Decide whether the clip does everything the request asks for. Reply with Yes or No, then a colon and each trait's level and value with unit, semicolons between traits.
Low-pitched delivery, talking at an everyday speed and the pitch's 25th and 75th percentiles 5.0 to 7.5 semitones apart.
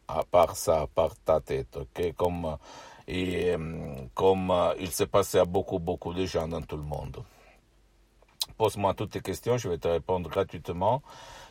No: very low, 90 Hz; average, 140 wpm; narrow, 2.6 semitones